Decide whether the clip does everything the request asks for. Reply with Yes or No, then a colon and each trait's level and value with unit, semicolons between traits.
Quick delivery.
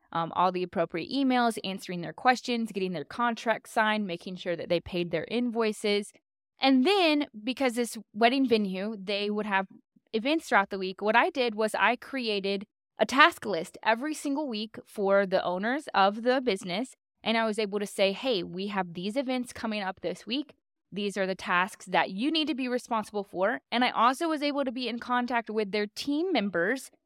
No: average, 195 wpm